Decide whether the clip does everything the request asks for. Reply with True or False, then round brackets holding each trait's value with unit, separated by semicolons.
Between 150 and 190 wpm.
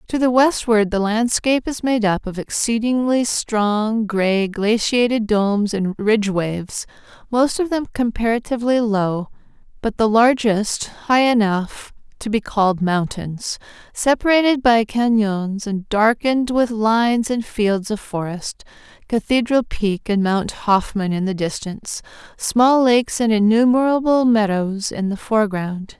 False (135 wpm)